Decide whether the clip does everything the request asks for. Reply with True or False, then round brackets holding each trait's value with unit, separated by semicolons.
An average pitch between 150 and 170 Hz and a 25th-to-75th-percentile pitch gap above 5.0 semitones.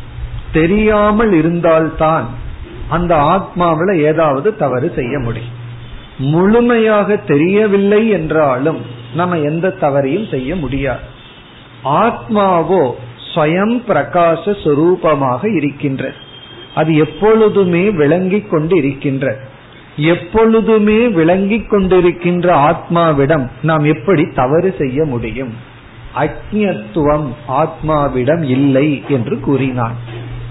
True (155 Hz; 5.6 semitones)